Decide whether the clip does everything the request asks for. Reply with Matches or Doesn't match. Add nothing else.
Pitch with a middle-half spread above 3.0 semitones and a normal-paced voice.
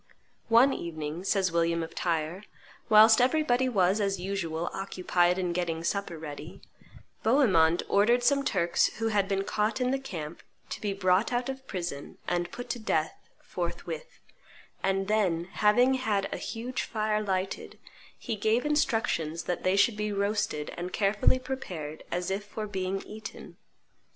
Matches